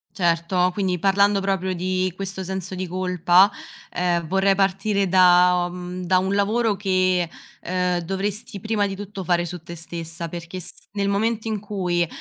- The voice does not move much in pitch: Yes, narrow, 1.8 semitones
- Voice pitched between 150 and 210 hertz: Yes, medium, 185 Hz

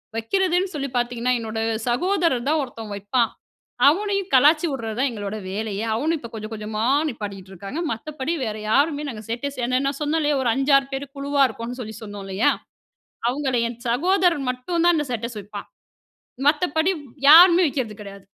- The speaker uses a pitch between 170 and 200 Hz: No, very high, 255 Hz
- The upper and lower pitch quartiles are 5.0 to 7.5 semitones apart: Yes, wide, 5.4 semitones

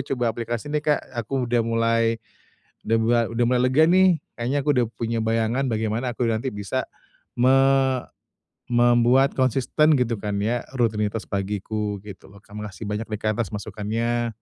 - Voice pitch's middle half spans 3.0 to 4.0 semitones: No, narrow, 2.5 semitones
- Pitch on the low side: Yes, low, 115 Hz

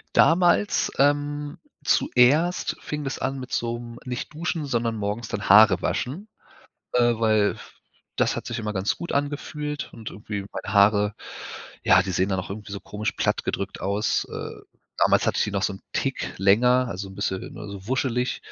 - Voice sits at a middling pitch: No, low, 115 Hz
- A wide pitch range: Yes, wide, 5.7 semitones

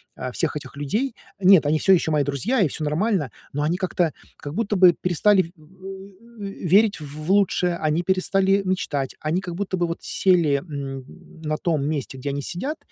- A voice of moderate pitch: Yes, medium, 175 Hz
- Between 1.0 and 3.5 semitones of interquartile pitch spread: No, average, 4.5 semitones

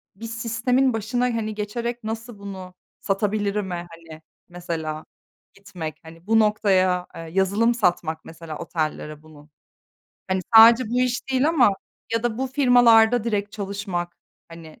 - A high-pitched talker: Yes, high, 205 Hz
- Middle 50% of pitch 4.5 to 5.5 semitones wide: Yes, average, 4.9 semitones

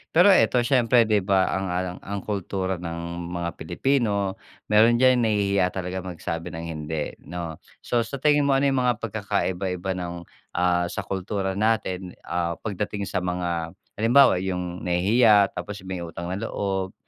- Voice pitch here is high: No, very low, 95 Hz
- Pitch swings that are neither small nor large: Yes, average, 3.5 semitones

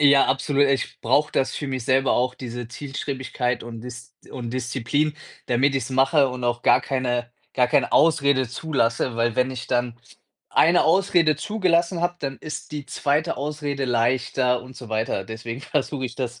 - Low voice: Yes, low, 130 Hz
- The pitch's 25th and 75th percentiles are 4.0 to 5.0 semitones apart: No, average, 2.9 semitones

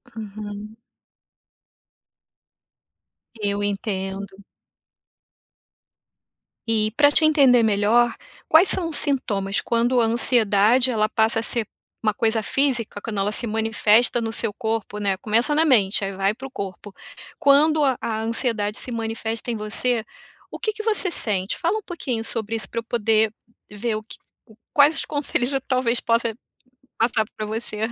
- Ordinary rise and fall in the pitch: Yes, average, 3.1 semitones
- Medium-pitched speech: No, high, 225 Hz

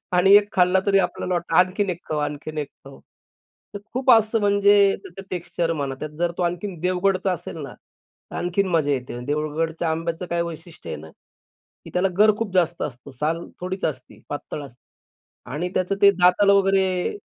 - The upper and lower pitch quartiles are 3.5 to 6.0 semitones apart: Yes, average, 3.8 semitones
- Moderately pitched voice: Yes, medium, 180 Hz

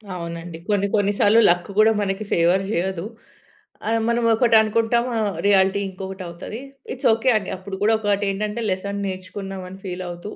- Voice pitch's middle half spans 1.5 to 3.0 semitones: Yes, narrow, 2.4 semitones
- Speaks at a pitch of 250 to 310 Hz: No, high, 195 Hz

